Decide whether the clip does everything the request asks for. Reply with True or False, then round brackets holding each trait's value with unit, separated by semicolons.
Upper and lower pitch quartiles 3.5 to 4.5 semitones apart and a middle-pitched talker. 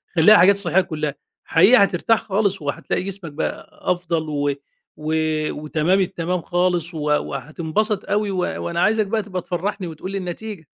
True (3.8 semitones; 180 Hz)